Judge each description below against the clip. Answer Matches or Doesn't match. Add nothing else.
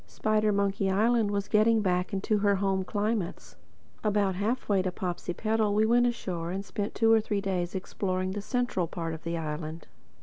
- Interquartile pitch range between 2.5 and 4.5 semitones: Matches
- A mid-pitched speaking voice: Doesn't match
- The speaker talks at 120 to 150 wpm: Doesn't match